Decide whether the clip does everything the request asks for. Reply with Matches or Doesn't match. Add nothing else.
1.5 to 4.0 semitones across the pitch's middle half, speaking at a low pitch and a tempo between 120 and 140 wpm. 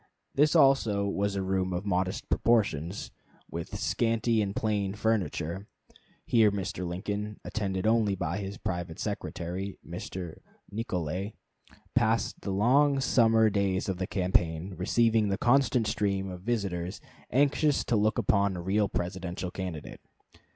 Matches